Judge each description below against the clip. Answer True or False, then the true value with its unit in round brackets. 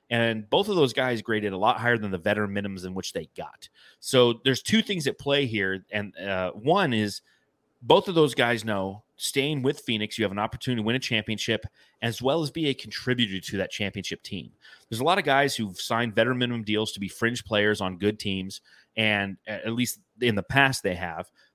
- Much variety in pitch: False (3.6 semitones)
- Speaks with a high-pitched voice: False (115 Hz)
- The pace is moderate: False (220 wpm)